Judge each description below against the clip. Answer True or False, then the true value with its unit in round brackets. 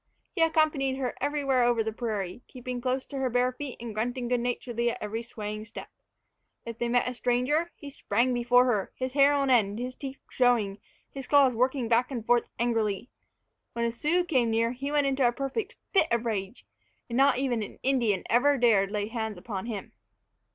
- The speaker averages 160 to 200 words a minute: True (195 wpm)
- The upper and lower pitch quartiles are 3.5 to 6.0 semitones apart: False (2.8 semitones)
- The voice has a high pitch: True (245 Hz)